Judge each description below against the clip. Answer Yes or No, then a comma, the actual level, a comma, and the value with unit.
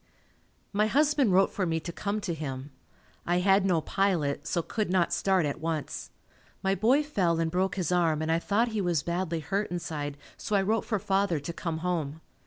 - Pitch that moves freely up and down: No, average, 3.6 semitones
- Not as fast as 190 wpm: No, average, 200 wpm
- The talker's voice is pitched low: No, medium, 180 Hz